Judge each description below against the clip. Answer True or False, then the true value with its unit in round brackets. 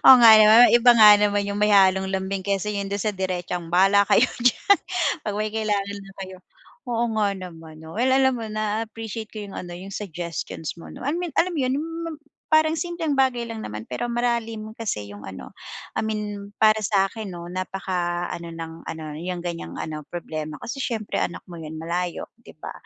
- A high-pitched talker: True (200 Hz)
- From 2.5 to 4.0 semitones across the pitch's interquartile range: False (4.4 semitones)